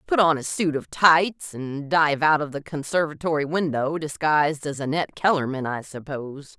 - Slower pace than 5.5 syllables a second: Yes, 5.0 syllables/s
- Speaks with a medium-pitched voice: Yes, medium, 150 Hz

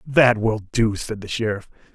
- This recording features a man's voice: Yes, male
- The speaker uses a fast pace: No, average, 185 wpm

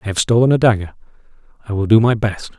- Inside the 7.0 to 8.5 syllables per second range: Yes, 7.1 syllables/s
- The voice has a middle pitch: No, low, 105 Hz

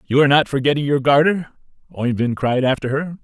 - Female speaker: No, male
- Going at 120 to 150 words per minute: No, average, 185 wpm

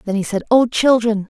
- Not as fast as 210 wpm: No, fast, 215 wpm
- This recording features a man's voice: No, female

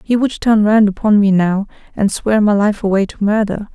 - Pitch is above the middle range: Yes, high, 210 Hz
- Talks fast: Yes, fast, 225 wpm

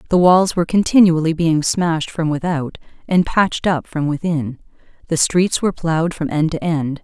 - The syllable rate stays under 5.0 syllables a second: No, 5.1 syllables/s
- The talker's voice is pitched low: No, medium, 165 Hz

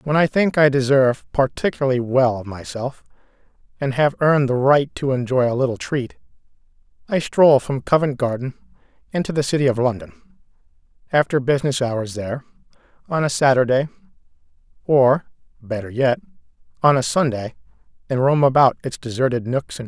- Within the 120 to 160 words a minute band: Yes, average, 150 wpm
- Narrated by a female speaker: No, male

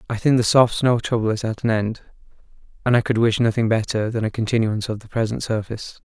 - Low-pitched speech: Yes, low, 115 Hz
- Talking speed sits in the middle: No, fast, 225 wpm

